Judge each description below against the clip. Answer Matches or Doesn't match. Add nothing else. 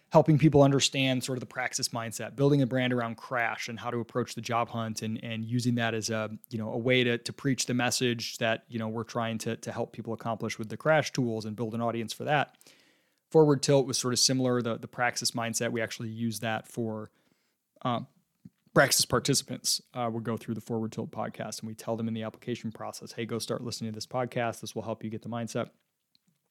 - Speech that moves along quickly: Matches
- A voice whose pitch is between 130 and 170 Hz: Doesn't match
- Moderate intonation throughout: Doesn't match